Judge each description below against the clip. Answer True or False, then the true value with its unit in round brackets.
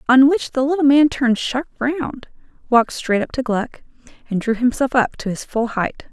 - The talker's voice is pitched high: True (255 Hz)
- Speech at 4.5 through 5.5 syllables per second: True (5.0 syllables/s)